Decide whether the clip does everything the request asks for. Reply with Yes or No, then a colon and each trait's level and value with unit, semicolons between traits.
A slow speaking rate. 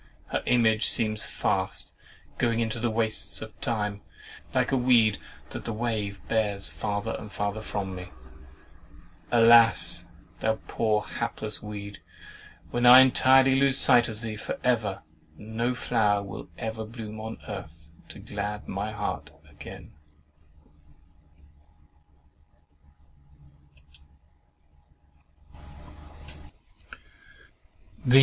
Yes: slow, 105 wpm